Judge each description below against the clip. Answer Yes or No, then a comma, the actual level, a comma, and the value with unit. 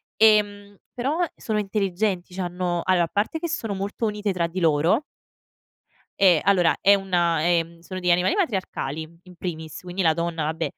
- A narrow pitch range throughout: No, average, 3.2 semitones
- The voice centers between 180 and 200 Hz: Yes, medium, 185 Hz